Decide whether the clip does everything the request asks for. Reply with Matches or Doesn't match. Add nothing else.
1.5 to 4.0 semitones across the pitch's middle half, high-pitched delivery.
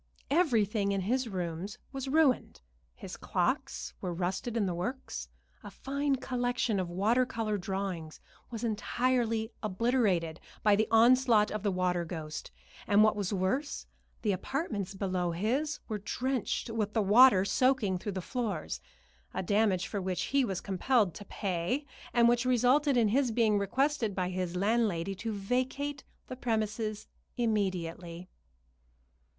Doesn't match